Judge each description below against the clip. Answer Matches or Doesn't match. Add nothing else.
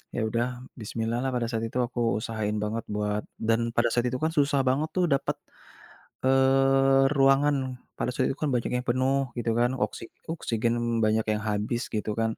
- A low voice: Matches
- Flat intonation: Doesn't match